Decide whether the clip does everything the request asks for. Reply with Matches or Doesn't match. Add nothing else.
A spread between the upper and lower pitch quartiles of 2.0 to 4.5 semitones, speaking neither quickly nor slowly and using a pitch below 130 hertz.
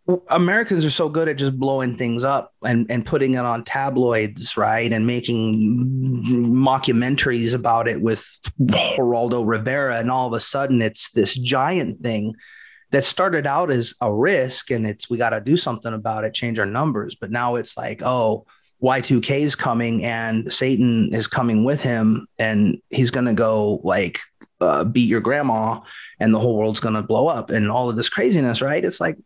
Matches